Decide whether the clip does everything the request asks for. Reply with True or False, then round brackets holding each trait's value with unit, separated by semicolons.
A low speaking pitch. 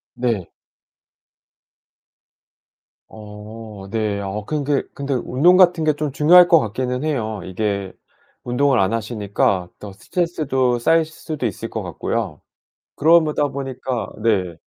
True (120 Hz)